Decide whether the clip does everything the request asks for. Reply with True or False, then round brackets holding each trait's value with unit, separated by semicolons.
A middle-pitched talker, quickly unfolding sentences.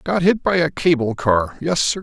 True (155 Hz; 235 wpm)